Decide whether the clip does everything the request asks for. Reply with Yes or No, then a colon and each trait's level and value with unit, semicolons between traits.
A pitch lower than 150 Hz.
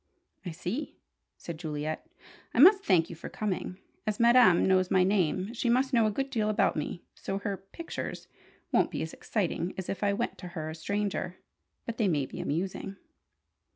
No: high, 195 Hz